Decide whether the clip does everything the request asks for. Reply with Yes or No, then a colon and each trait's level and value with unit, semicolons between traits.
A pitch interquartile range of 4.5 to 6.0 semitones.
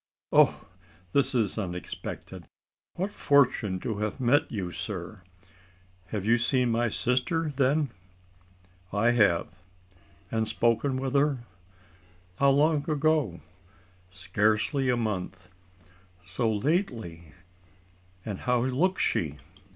Yes: wide, 5.4 semitones